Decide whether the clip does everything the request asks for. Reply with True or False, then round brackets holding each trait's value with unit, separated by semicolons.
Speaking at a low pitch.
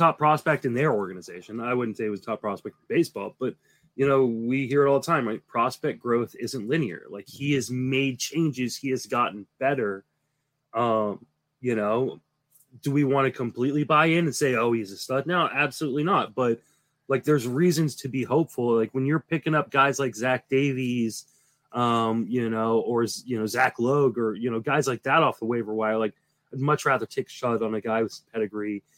True (130 Hz)